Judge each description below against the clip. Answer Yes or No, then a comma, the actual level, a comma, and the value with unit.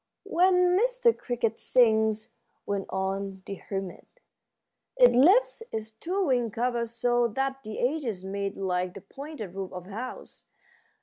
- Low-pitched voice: No, high, 230 Hz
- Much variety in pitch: Yes, wide, 5.7 semitones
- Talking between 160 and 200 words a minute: No, average, 140 wpm